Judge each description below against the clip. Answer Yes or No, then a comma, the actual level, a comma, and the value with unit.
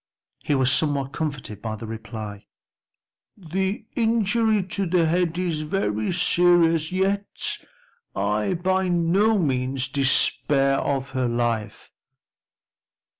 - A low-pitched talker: No, medium, 155 Hz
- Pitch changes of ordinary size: No, wide, 6.4 semitones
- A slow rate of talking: Yes, slow, 110 wpm